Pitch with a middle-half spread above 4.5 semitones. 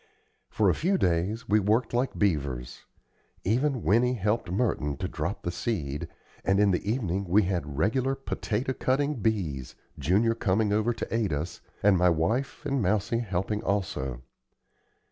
Yes: average, 5.0 semitones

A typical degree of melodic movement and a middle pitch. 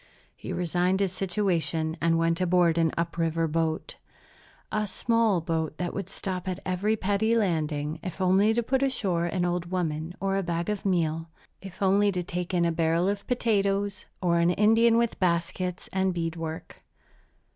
Yes: average, 3.0 semitones; medium, 180 Hz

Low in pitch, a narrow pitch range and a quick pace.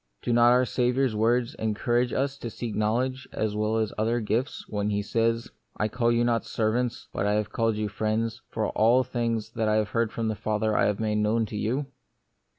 Yes: low, 115 Hz; narrow, 1.9 semitones; fast, 225 wpm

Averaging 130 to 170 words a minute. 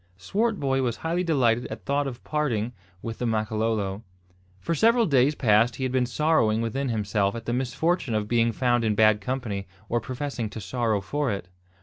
No: average, 185 wpm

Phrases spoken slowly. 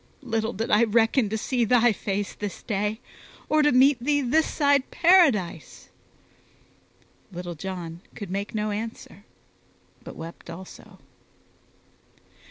Yes: slow, 125 wpm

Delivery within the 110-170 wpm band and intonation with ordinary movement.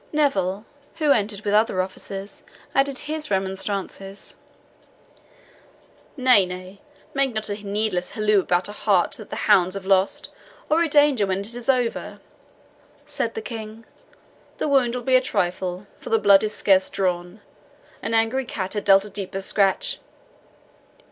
Yes: average, 155 wpm; average, 4.2 semitones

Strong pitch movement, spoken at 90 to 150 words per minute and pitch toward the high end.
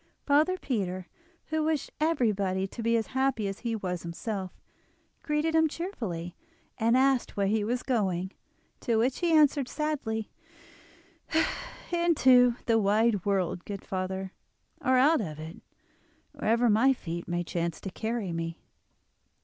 Yes: wide, 6.0 semitones; average, 140 wpm; high, 225 Hz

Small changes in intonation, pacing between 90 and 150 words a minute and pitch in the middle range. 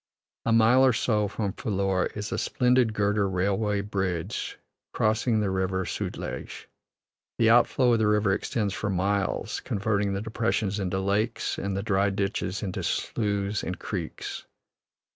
No: narrow, 2.3 semitones; average, 145 wpm; low, 100 Hz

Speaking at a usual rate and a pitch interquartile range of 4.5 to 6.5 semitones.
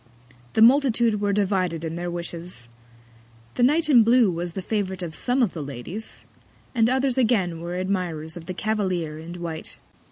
Yes: average, 170 wpm; average, 5.0 semitones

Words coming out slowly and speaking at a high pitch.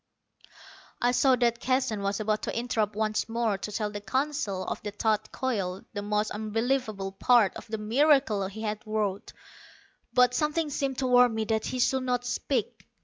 No: average, 180 wpm; high, 220 Hz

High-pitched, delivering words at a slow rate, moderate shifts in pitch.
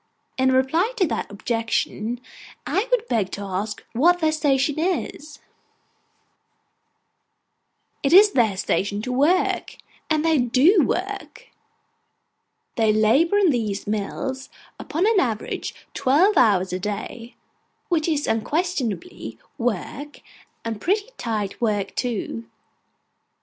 No: very high, 260 Hz; slow, 115 wpm; wide, 7.5 semitones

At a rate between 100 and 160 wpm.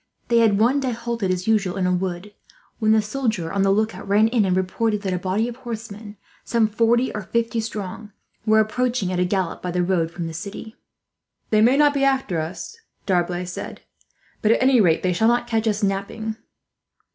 No: fast, 205 wpm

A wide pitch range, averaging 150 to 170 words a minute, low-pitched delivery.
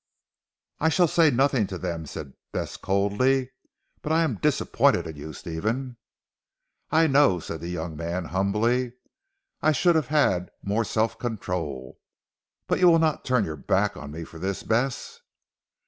Yes: wide, 8.1 semitones; average, 160 wpm; low, 105 Hz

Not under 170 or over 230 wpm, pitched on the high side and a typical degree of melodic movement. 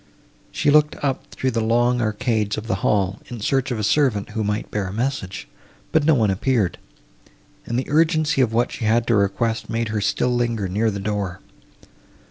No: average, 195 wpm; low, 115 Hz; average, 3.5 semitones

